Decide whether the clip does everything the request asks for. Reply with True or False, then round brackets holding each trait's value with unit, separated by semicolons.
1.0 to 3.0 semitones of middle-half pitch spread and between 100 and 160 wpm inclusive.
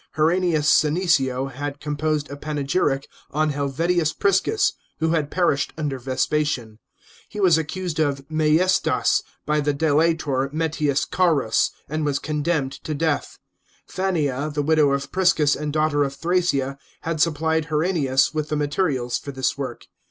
True (2.5 semitones; 140 wpm)